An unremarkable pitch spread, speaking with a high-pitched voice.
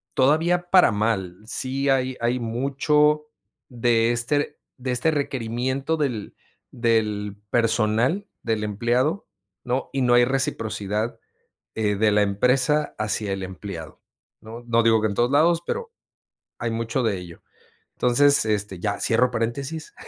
No: average, 4.1 semitones; low, 120 Hz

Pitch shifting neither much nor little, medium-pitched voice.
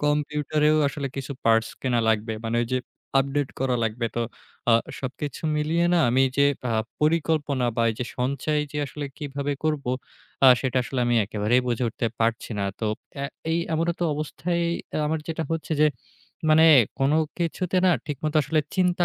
Yes: average, 3.7 semitones; medium, 145 Hz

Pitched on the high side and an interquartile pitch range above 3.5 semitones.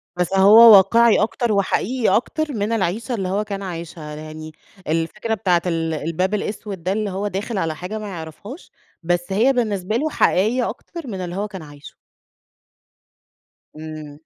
Yes: high, 195 Hz; average, 4.5 semitones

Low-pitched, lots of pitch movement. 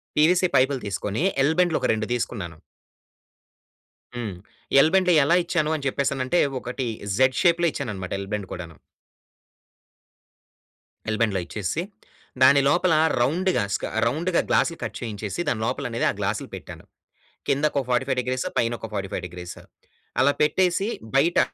Yes: low, 130 Hz; wide, 7.3 semitones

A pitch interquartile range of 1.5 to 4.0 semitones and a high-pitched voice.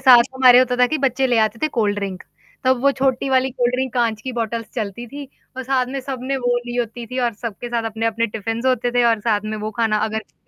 Yes: narrow, 2.4 semitones; high, 240 Hz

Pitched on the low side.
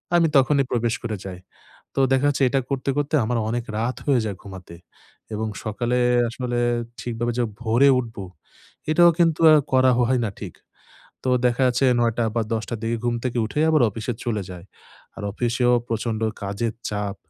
Yes: low, 120 Hz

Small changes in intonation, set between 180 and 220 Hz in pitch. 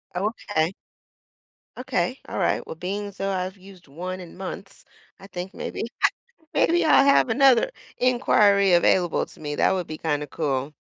No: average, 3.5 semitones; high, 190 Hz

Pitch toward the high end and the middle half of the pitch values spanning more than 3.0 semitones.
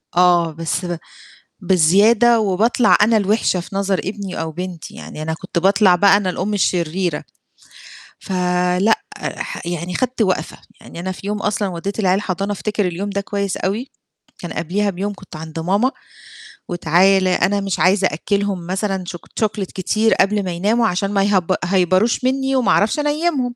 No: high, 195 Hz; average, 2.7 semitones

